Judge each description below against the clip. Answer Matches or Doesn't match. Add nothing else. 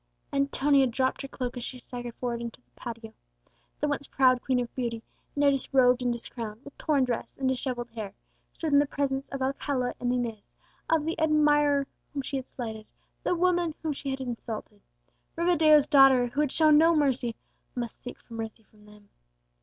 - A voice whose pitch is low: Doesn't match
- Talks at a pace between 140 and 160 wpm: Doesn't match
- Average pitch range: Matches